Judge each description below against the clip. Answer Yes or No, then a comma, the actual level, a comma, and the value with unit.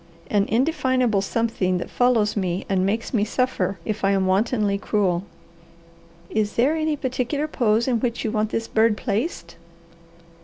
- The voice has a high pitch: Yes, high, 220 Hz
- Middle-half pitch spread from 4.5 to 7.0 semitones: No, average, 3.9 semitones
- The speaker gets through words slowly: No, average, 155 wpm